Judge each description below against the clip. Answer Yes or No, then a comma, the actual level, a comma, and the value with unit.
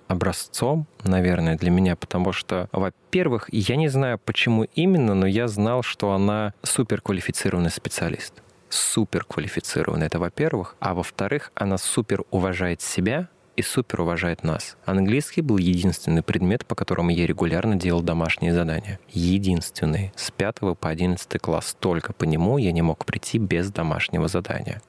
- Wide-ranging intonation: No, average, 4.4 semitones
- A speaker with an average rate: Yes, average, 140 wpm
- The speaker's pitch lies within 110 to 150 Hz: No, very low, 95 Hz